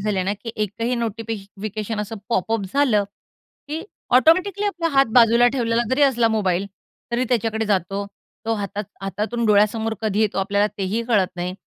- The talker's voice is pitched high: Yes, high, 220 Hz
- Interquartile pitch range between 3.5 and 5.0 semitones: No, average, 2.8 semitones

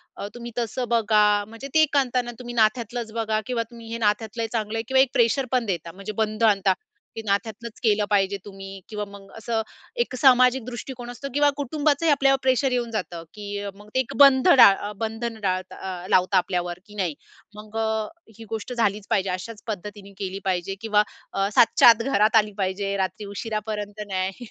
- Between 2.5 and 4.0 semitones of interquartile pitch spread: Yes, average, 3.2 semitones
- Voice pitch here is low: No, high, 215 Hz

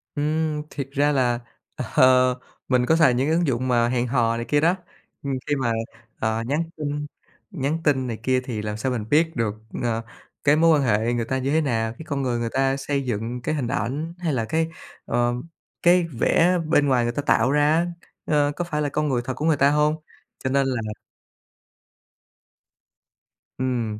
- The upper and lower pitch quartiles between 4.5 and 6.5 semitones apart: No, average, 3.8 semitones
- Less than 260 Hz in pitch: Yes, low, 135 Hz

